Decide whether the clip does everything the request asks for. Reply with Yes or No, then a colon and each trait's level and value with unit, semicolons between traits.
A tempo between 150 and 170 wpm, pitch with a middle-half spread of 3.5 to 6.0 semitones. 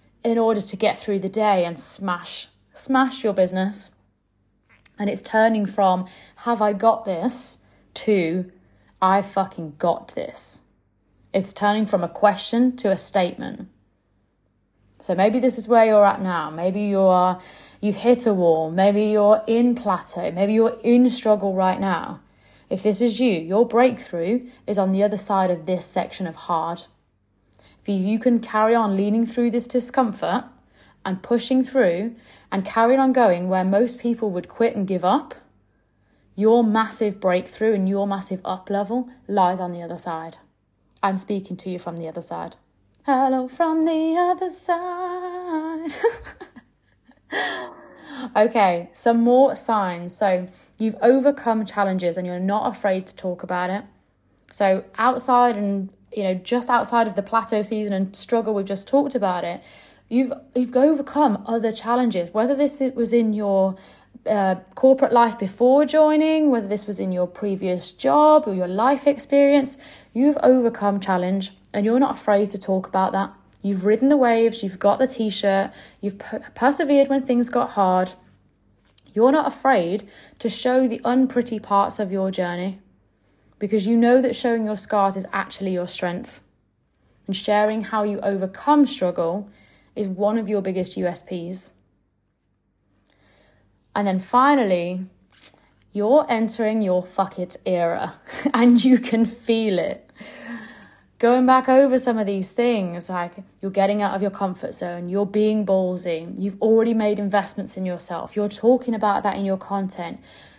Yes: average, 155 wpm; average, 4.4 semitones